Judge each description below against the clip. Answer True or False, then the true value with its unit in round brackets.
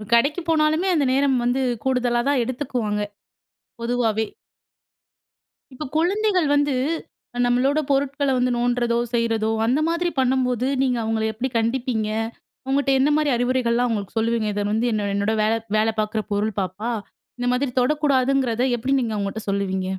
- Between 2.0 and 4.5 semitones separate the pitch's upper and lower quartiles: True (3.6 semitones)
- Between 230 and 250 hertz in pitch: True (245 Hz)